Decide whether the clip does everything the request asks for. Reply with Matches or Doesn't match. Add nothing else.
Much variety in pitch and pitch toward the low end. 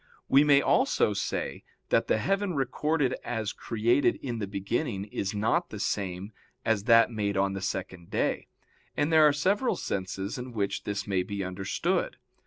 Matches